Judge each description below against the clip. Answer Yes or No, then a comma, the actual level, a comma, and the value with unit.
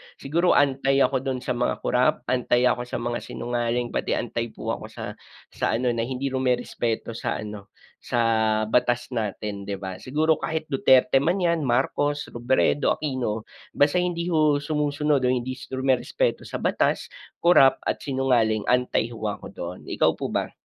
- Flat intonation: No, average, 3.4 semitones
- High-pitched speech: No, low, 130 Hz